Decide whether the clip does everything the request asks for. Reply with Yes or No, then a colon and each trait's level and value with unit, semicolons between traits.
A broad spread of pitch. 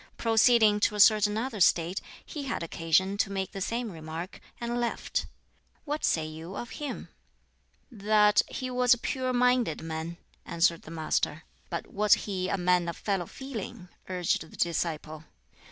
Yes: wide, 5.8 semitones